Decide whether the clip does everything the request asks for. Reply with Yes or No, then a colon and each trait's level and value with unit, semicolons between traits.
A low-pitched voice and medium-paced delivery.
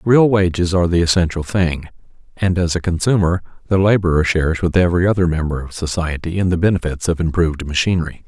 Yes: very low, 85 Hz; average, 180 wpm